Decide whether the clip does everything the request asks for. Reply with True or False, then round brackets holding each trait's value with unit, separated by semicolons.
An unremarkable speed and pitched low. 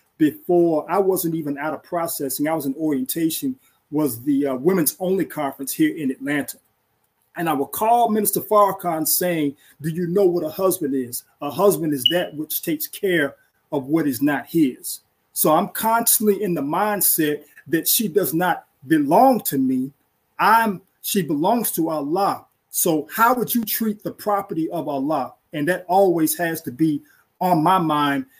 False (175 wpm; 175 Hz)